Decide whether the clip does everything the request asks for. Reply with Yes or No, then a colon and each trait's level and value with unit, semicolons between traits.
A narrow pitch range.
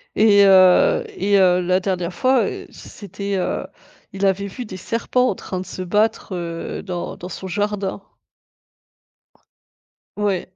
Yes: narrow, 2.1 semitones